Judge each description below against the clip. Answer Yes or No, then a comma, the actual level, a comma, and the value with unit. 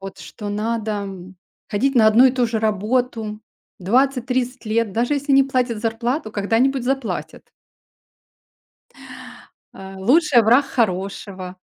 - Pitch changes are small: No, average, 3.8 semitones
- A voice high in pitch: Yes, high, 230 Hz